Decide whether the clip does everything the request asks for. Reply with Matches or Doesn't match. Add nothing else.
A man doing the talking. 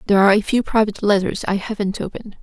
Doesn't match